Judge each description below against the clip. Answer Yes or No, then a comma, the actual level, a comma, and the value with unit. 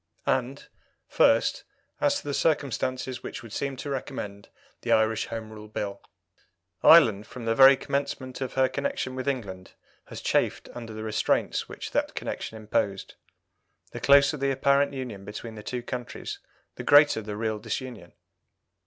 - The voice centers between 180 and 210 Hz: No, low, 120 Hz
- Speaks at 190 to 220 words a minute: No, average, 155 wpm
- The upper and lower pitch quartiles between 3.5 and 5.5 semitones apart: Yes, average, 4.1 semitones